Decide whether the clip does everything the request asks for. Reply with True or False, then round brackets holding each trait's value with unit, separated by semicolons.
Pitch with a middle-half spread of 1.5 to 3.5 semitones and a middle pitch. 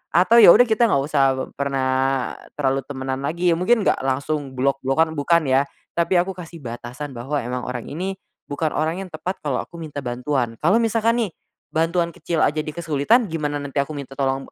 False (4.2 semitones; 150 Hz)